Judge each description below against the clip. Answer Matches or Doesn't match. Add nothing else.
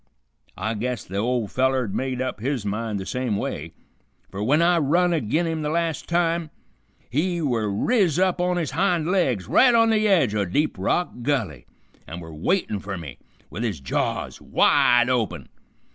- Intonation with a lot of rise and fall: Matches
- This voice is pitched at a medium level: Doesn't match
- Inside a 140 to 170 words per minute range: Doesn't match